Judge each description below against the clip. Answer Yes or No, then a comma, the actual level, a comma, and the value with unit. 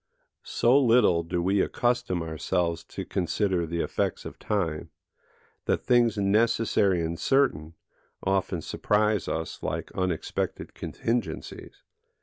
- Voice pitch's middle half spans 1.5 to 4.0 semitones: No, average, 5.1 semitones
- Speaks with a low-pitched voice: Yes, very low, 95 Hz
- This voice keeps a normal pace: No, slow, 115 wpm